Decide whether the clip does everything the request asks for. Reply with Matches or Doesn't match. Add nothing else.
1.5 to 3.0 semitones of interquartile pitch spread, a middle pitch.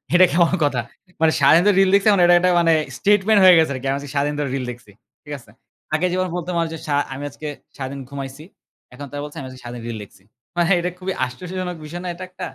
Doesn't match